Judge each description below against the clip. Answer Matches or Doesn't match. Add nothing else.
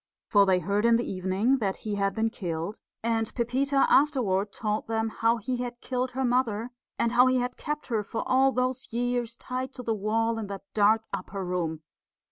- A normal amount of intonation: Matches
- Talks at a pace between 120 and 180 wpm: Doesn't match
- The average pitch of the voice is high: Matches